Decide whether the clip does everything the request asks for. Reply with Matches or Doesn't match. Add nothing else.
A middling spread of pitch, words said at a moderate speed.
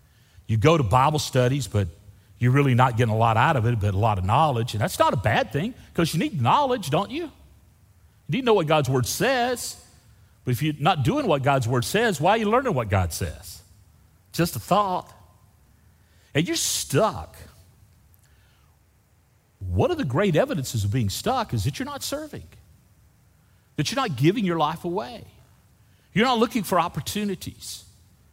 Doesn't match